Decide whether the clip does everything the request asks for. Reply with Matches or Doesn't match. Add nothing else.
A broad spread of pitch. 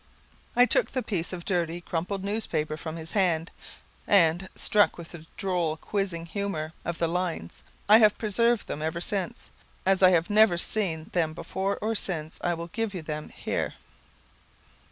Doesn't match